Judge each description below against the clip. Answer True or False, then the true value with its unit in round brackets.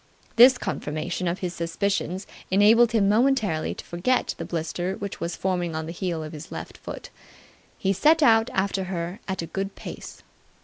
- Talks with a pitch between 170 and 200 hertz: True (190 Hz)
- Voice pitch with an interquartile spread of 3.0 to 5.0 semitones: True (3.6 semitones)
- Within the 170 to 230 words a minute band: True (175 wpm)